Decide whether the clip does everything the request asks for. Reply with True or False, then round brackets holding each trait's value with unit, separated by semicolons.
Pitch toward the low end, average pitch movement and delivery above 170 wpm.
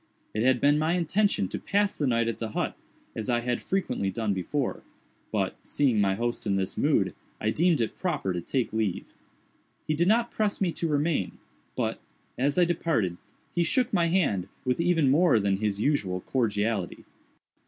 False (130 Hz; 8.1 semitones; 185 wpm)